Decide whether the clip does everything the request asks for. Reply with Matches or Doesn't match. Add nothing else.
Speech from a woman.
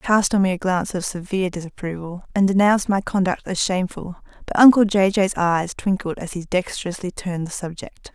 Matches